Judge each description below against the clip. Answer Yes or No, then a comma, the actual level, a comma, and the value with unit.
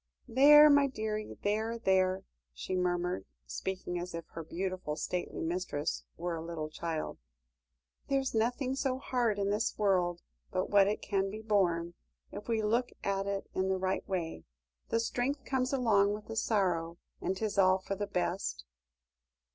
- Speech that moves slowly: No, average, 165 wpm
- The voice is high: Yes, high, 195 Hz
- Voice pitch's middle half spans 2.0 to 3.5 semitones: No, average, 4.0 semitones